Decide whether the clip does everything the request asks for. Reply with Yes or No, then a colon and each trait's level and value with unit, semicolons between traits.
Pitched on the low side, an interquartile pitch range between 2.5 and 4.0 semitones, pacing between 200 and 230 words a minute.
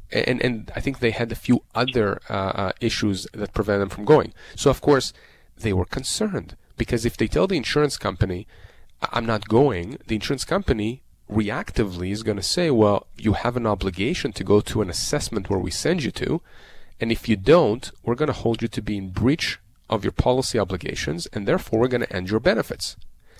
Yes: low, 110 Hz; average, 3.5 semitones; fast, 205 wpm